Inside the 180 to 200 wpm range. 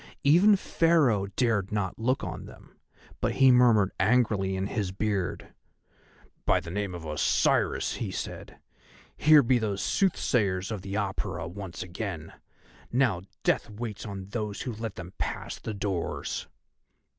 No: average, 145 wpm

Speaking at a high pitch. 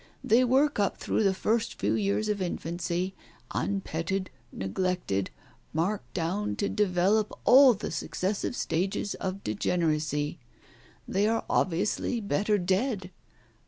Yes: high, 195 Hz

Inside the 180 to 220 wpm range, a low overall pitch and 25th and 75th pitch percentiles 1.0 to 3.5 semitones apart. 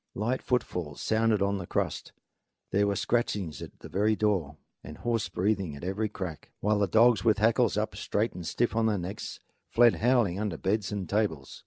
Yes: average, 190 wpm; low, 105 Hz; average, 3.1 semitones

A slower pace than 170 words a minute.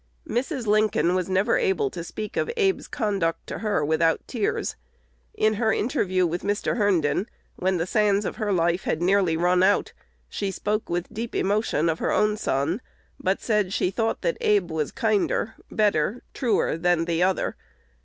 No: average, 175 wpm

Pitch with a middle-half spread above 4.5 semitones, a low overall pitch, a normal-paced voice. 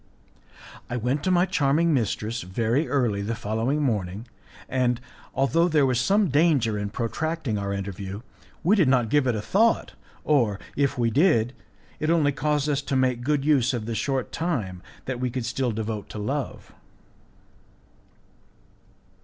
Yes: average, 5.0 semitones; low, 125 Hz; average, 160 wpm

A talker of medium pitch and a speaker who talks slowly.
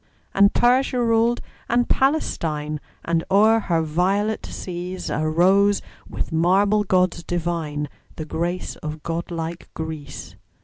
Yes: medium, 175 Hz; slow, 120 wpm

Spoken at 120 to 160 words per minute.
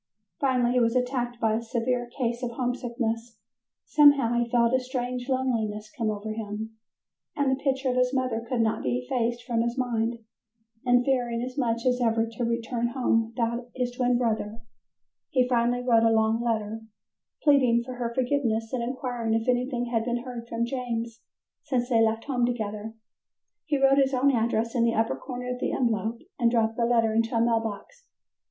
No: average, 185 wpm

